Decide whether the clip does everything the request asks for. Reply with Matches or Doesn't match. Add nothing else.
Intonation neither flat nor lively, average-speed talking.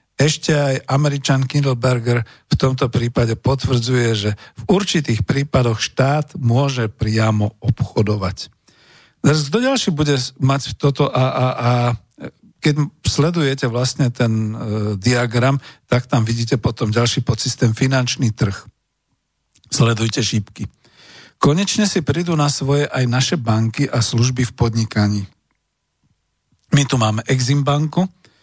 Matches